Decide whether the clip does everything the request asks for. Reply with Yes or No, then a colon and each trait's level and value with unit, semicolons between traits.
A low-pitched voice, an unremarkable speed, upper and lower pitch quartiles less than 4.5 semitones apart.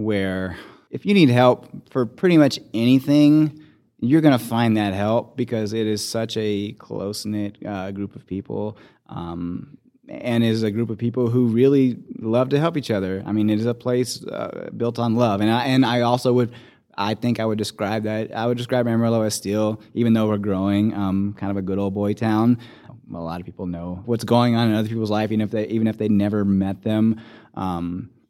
No: low, 110 Hz; fast, 215 wpm; average, 2.7 semitones